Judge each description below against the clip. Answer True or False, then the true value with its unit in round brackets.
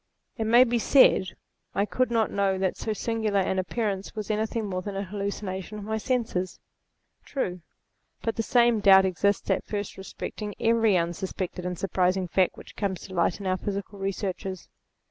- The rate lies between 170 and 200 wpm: True (180 wpm)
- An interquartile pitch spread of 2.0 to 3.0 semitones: True (2.7 semitones)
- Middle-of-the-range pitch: False (200 Hz)